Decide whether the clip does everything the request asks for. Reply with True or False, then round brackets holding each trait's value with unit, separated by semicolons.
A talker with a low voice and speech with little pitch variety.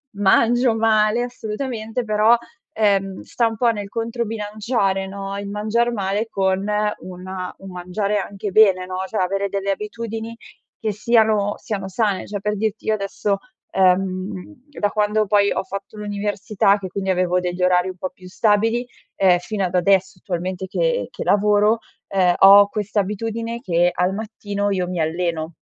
False (205 Hz; 2.3 semitones)